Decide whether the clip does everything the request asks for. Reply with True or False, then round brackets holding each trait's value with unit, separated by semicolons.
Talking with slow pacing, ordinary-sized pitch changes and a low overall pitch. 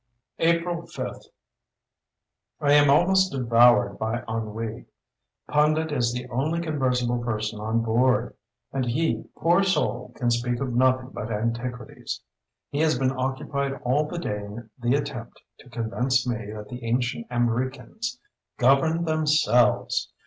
True (130 wpm; 3.9 semitones; 125 Hz)